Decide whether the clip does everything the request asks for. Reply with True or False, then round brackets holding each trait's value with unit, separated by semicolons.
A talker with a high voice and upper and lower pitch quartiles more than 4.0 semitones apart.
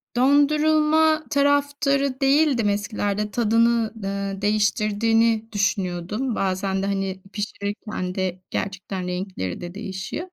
True (210 Hz; 5.6 semitones)